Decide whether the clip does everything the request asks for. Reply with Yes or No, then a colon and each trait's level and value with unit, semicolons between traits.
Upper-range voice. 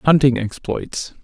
No: low, 130 Hz